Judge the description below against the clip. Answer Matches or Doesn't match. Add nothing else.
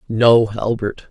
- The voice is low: Matches